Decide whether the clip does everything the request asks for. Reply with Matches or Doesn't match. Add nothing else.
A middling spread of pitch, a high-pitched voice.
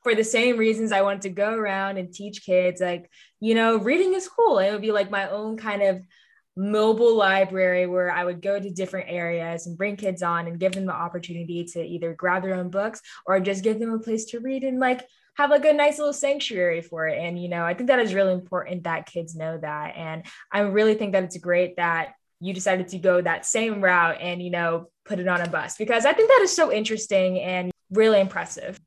Matches